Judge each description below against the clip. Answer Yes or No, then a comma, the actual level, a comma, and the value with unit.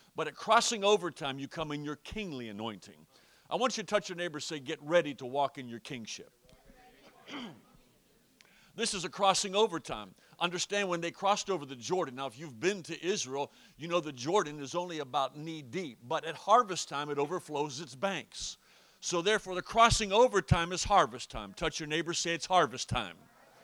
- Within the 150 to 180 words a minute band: No, average, 200 wpm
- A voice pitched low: No, medium, 170 Hz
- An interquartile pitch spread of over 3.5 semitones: Yes, average, 5.0 semitones